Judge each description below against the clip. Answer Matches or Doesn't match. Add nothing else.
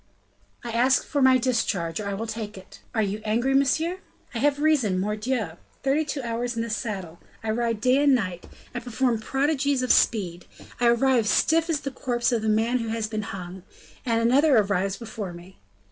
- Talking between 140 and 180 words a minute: Doesn't match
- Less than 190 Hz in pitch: Doesn't match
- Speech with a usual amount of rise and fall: Matches